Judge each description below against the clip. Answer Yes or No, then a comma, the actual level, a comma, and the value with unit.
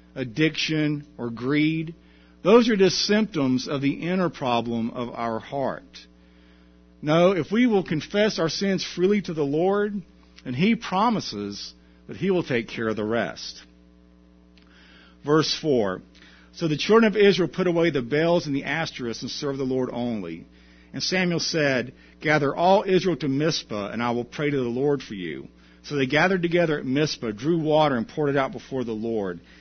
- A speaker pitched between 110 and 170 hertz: Yes, medium, 140 Hz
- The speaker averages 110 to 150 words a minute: No, average, 175 wpm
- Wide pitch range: Yes, wide, 7.9 semitones